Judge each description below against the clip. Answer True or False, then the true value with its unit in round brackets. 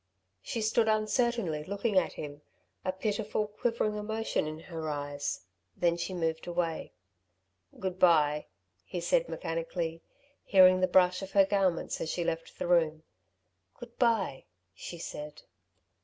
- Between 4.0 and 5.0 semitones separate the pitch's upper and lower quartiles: True (4.5 semitones)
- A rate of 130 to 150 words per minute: True (140 wpm)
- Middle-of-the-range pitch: True (180 Hz)